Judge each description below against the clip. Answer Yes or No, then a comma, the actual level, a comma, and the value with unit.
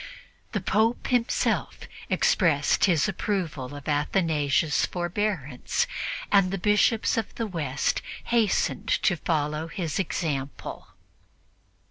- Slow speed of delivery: Yes, slow, 100 wpm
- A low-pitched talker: No, medium, 175 Hz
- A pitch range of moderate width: No, wide, 5.8 semitones